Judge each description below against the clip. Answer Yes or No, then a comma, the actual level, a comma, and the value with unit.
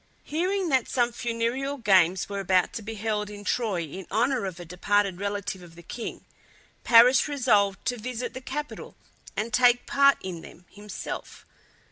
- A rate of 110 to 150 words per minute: No, average, 165 wpm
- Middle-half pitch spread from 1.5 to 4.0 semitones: No, average, 4.5 semitones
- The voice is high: Yes, high, 215 Hz